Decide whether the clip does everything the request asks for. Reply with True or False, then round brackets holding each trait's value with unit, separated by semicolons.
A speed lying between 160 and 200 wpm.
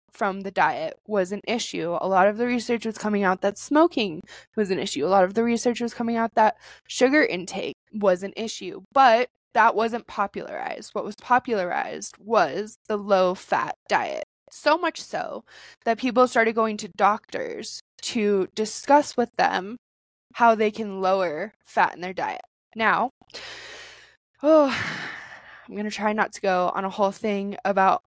True (170 wpm)